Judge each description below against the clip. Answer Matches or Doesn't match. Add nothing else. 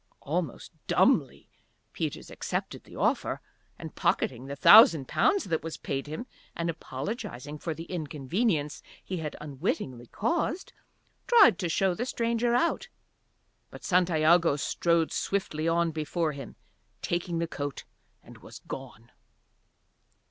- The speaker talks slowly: Matches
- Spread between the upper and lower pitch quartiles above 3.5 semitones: Matches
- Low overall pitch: Doesn't match